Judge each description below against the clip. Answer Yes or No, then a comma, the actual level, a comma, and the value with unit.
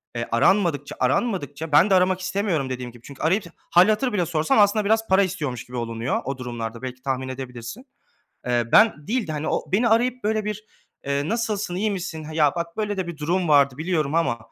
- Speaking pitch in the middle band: Yes, medium, 165 Hz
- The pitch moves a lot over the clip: Yes, wide, 7.1 semitones